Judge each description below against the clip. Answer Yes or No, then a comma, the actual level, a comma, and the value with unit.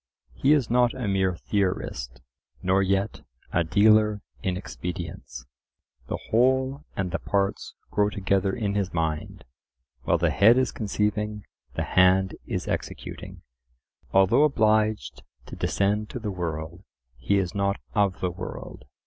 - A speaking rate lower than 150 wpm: Yes, average, 140 wpm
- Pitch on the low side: Yes, low, 100 Hz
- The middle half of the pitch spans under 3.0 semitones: Yes, narrow, 2.6 semitones